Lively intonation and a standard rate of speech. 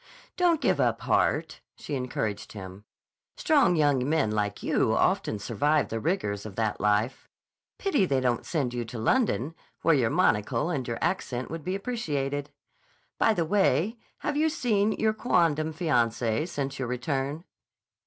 Yes: wide, 7.8 semitones; average, 155 wpm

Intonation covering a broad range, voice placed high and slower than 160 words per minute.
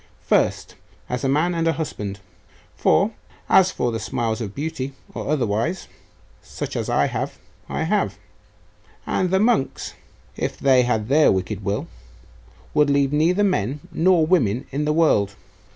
No: wide, 6.4 semitones; medium, 140 Hz; average, 150 wpm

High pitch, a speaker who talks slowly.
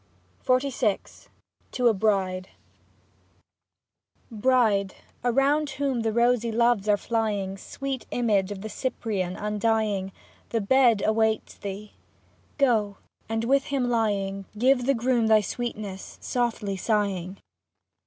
Yes: high, 220 Hz; slow, 125 wpm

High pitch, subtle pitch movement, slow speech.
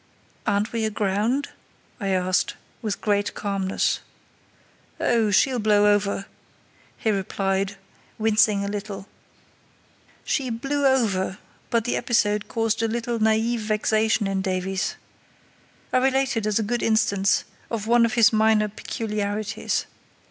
Yes: high, 215 Hz; narrow, 2.2 semitones; slow, 125 wpm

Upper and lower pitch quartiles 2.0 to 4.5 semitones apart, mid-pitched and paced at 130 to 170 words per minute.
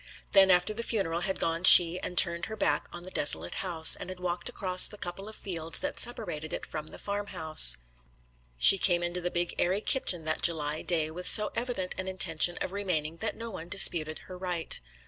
No: average, 2.9 semitones; medium, 180 Hz; fast, 205 wpm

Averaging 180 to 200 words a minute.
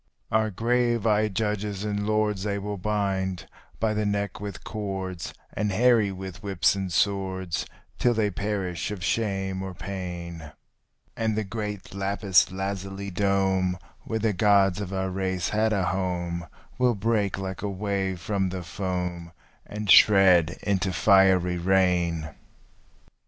No: average, 140 wpm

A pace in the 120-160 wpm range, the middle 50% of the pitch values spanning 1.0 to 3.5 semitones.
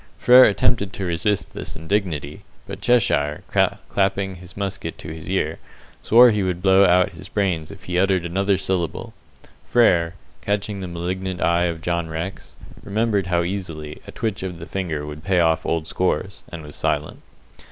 No: average, 170 wpm; average, 2.9 semitones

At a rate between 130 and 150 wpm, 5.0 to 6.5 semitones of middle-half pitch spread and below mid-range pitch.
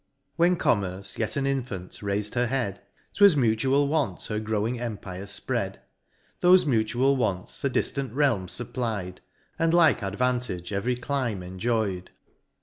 Yes: slow, 135 wpm; wide, 5.4 semitones; low, 115 Hz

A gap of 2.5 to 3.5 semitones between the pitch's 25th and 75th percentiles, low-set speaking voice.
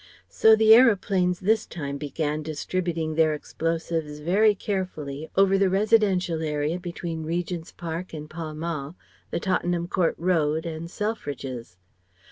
No: average, 3.2 semitones; medium, 170 Hz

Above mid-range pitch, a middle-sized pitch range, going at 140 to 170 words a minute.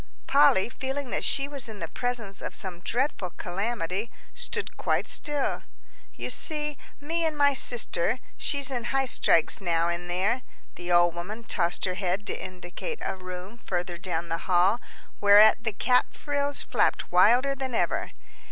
No: high, 215 Hz; wide, 7.0 semitones; average, 160 wpm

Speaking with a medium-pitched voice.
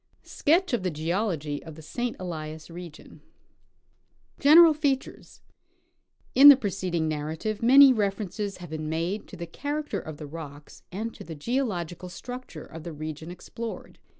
Yes: medium, 180 Hz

